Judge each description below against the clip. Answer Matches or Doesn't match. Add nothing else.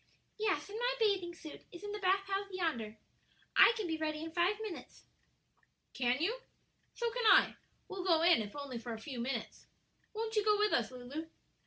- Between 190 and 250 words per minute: Matches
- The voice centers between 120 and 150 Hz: Doesn't match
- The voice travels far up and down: Matches